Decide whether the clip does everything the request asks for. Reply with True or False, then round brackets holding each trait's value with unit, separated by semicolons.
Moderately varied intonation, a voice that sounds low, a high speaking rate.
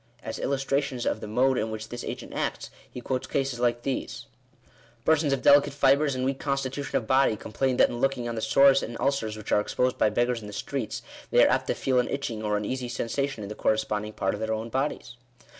True (3.7 semitones; 125 Hz; 235 wpm)